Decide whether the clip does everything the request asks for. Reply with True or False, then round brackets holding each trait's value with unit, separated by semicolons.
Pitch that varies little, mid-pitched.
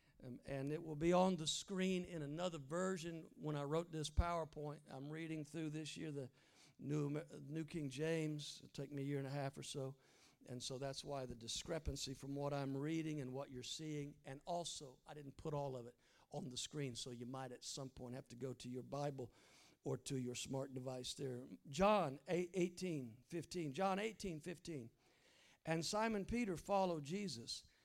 False (3.5 semitones; 145 Hz)